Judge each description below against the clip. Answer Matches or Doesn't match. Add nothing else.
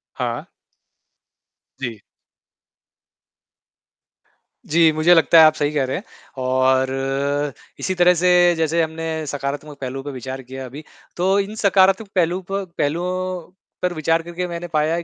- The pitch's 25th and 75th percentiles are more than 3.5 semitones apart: Matches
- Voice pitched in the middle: Matches